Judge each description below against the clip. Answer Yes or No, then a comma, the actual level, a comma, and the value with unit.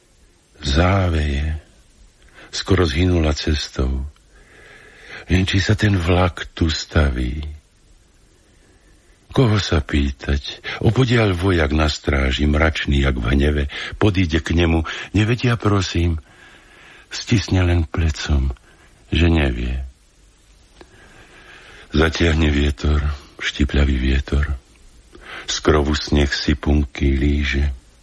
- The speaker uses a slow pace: Yes, slow, 90 wpm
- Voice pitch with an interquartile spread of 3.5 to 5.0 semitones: Yes, average, 3.9 semitones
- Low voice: Yes, very low, 75 Hz